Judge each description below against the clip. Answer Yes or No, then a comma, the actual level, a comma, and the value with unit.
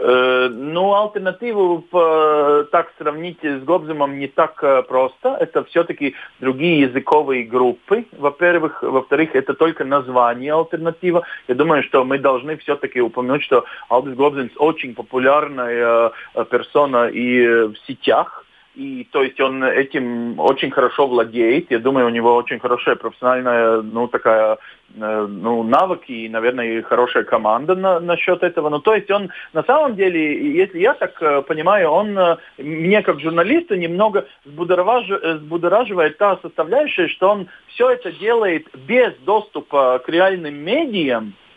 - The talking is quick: No, average, 130 wpm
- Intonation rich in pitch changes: Yes, wide, 6.5 semitones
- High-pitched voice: No, medium, 150 Hz